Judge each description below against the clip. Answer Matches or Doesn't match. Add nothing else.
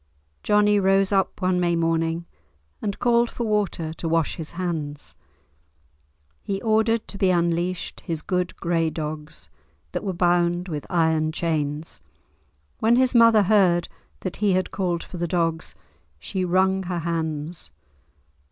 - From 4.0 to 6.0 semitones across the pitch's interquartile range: Doesn't match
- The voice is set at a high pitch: Doesn't match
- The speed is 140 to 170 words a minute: Matches